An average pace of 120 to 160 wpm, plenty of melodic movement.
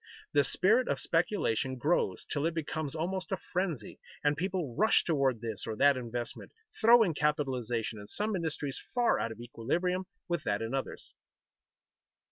Yes: average, 155 wpm; wide, 7.0 semitones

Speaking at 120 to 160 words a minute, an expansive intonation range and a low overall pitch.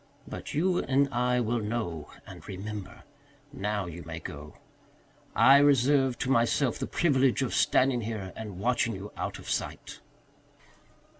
No: average, 145 wpm; average, 4.9 semitones; low, 120 Hz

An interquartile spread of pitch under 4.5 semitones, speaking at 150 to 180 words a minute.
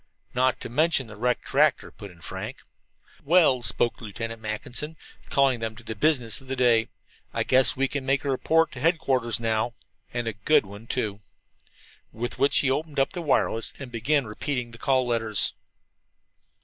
Yes: average, 3.5 semitones; average, 175 wpm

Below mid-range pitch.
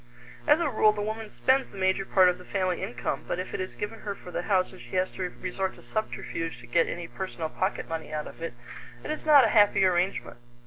No: high, 190 Hz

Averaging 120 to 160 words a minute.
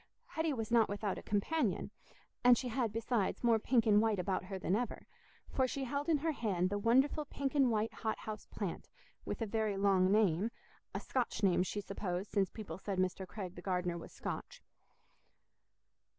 No: average, 185 wpm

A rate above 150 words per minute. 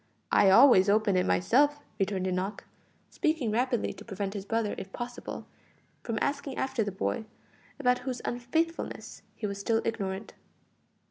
No: average, 145 wpm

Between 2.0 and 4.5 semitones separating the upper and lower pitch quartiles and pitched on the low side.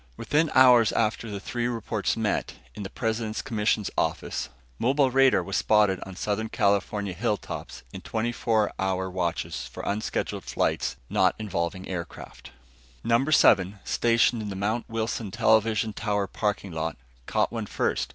Yes: average, 2.9 semitones; low, 110 Hz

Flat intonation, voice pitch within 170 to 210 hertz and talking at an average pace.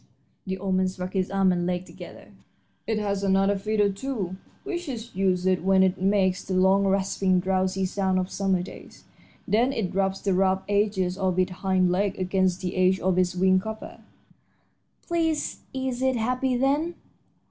Yes: narrow, 2.0 semitones; high, 190 Hz; average, 175 wpm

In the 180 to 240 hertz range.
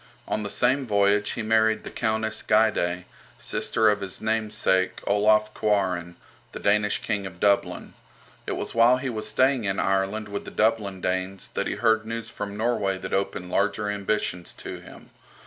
No: low, 105 Hz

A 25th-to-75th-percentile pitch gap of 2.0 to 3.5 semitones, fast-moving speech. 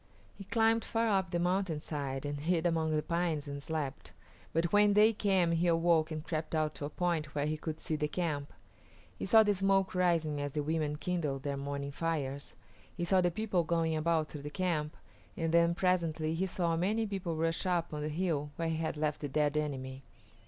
Yes: average, 3.0 semitones; fast, 210 wpm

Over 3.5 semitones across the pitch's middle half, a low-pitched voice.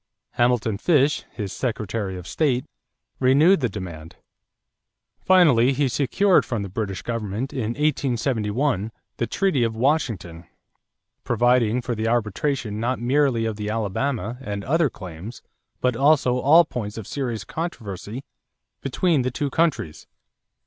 Yes: average, 4.6 semitones; low, 120 Hz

